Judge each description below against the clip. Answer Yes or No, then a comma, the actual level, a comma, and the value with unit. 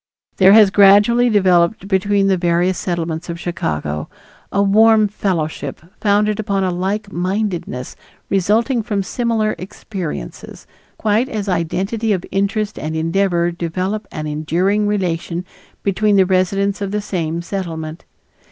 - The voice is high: Yes, high, 195 Hz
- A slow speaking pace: Yes, slow, 130 wpm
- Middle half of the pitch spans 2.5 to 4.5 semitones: Yes, average, 3.3 semitones